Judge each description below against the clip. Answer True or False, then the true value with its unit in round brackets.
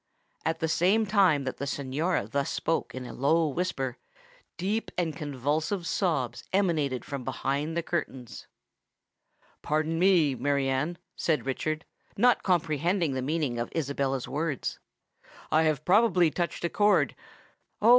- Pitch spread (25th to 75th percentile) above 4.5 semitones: False (4.2 semitones)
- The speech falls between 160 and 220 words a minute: False (140 wpm)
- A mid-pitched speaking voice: True (155 Hz)